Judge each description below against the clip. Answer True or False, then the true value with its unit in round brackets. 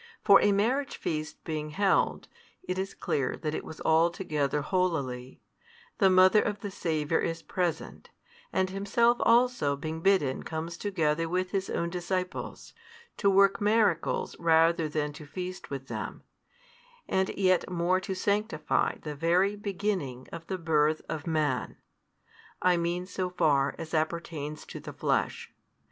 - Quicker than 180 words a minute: False (145 wpm)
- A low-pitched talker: False (170 Hz)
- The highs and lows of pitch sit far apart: False (3.7 semitones)